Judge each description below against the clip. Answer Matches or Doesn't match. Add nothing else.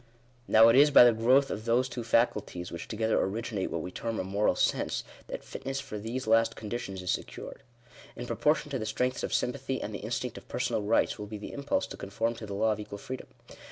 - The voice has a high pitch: Doesn't match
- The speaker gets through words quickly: Matches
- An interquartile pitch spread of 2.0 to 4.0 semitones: Matches